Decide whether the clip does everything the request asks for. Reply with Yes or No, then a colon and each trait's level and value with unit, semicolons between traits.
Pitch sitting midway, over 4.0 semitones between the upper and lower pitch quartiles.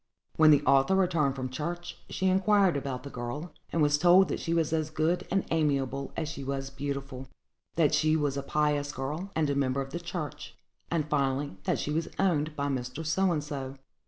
No: medium, 150 Hz; average, 3.1 semitones